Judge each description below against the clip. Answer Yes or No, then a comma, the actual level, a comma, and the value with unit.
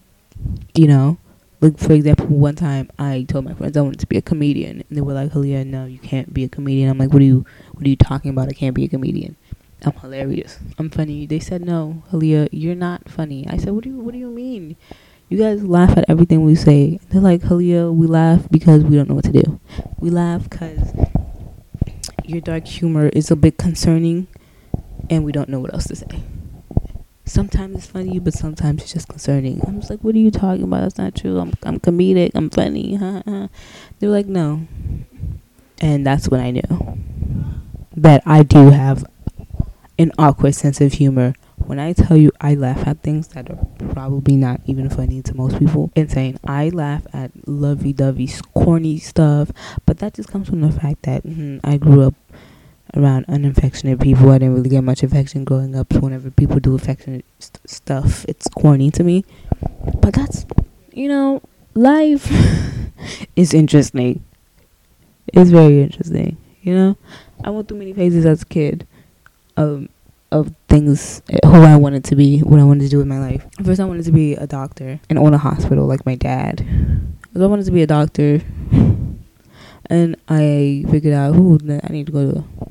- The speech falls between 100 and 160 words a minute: No, average, 195 wpm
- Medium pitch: Yes, medium, 145 Hz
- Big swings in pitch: No, average, 3.7 semitones